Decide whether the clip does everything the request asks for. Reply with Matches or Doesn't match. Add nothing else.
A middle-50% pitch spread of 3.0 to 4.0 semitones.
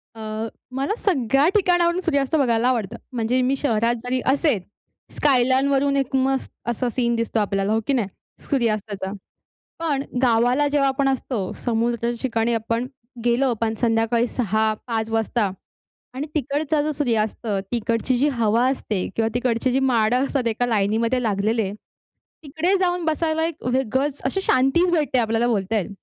Matches